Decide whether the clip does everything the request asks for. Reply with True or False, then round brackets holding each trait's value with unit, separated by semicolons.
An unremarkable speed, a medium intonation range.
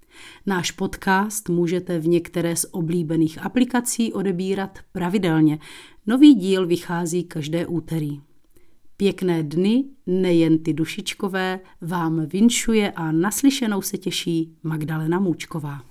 False (105 wpm; 3.2 semitones)